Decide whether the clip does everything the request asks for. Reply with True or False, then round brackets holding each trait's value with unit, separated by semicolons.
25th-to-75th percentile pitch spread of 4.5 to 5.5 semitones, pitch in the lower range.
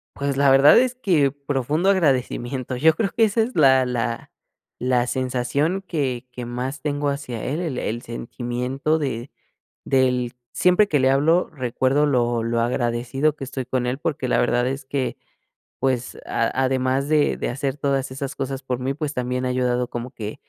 False (2.7 semitones; 130 Hz)